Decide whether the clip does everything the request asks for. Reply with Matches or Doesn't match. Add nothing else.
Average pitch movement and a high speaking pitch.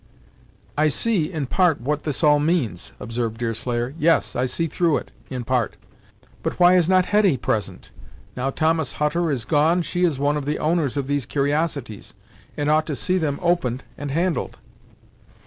Doesn't match